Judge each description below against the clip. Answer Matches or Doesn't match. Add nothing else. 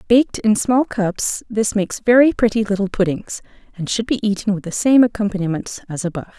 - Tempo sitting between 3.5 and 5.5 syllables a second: Doesn't match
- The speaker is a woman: Matches